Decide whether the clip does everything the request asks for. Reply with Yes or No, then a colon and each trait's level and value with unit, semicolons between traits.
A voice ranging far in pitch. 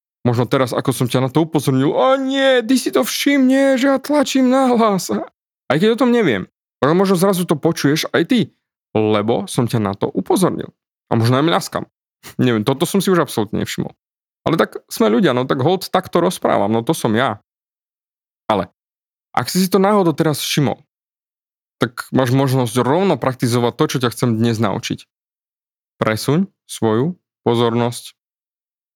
Yes: wide, 8.8 semitones